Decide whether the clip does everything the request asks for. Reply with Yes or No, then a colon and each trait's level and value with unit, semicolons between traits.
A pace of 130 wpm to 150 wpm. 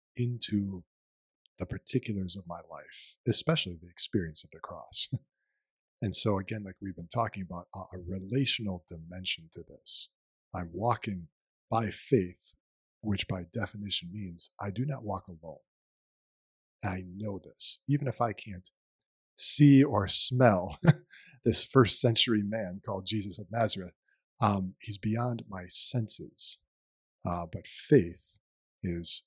Yes: slow, 135 wpm